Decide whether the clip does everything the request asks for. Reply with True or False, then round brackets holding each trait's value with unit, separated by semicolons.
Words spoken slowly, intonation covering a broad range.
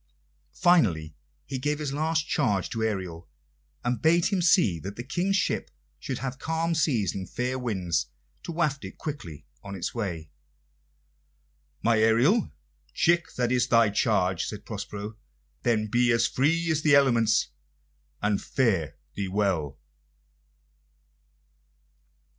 True (130 wpm; 7.0 semitones)